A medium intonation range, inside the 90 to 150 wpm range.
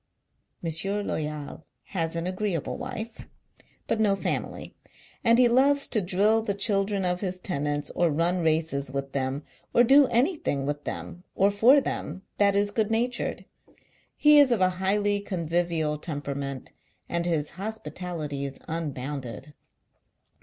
No: wide, 5.9 semitones; average, 145 wpm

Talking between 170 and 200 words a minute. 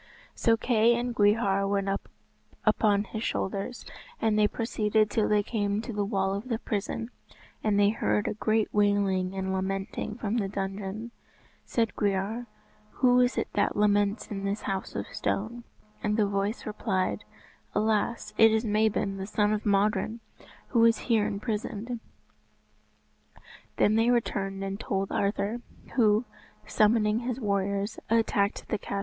No: average, 150 wpm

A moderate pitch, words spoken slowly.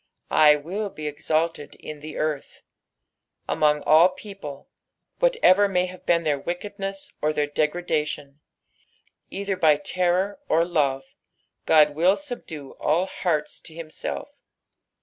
Yes: medium, 160 Hz; slow, 130 wpm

